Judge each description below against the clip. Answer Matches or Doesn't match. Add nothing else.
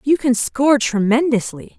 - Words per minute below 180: Matches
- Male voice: Doesn't match